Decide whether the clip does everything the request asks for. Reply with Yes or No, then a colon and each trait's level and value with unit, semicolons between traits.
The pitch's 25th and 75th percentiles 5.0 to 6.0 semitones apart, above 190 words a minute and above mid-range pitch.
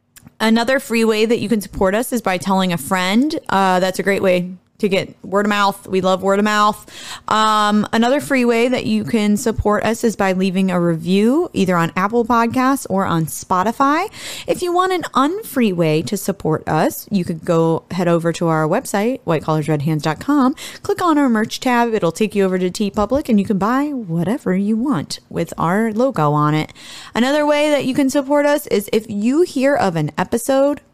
Yes: wide, 5.4 semitones; average, 200 wpm; high, 210 Hz